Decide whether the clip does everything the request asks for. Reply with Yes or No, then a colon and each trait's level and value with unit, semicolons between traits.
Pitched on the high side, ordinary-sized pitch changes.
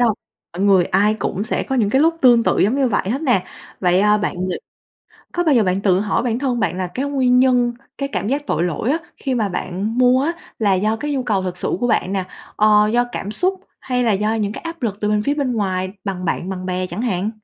Yes: high, 215 Hz; average, 4.8 semitones